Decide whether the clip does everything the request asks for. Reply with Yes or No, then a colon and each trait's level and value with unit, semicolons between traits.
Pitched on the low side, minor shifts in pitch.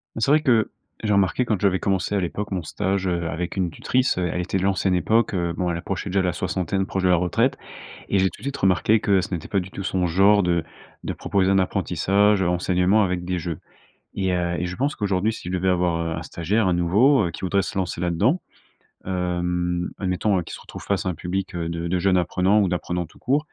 Yes: very low, 95 Hz; narrow, 2.1 semitones